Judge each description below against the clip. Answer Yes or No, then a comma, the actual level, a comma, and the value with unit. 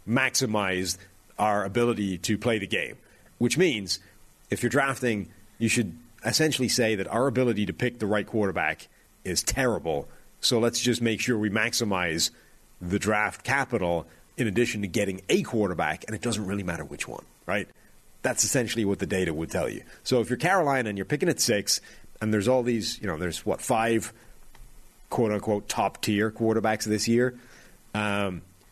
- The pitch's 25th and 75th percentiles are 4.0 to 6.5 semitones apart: No, average, 3.1 semitones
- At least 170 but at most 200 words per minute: Yes, average, 175 wpm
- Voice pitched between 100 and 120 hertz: Yes, low, 110 Hz